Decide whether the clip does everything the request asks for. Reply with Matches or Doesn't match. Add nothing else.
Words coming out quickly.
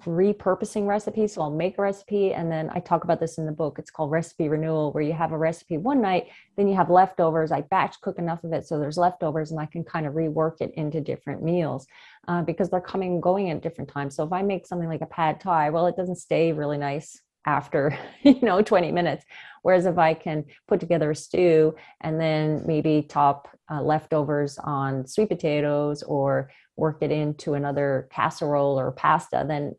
Matches